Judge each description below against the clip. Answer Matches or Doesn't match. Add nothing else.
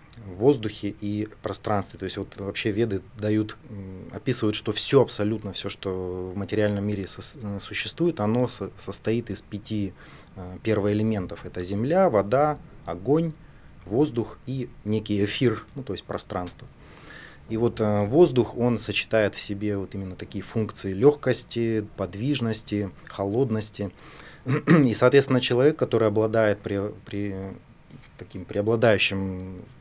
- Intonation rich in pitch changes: Doesn't match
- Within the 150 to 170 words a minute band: Doesn't match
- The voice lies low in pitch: Matches